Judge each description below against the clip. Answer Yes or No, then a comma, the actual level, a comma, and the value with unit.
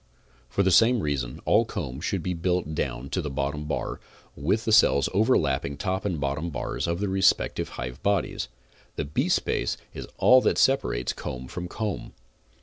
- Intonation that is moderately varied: No, wide, 5.8 semitones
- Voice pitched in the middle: No, very low, 85 Hz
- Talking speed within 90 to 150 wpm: No, average, 170 wpm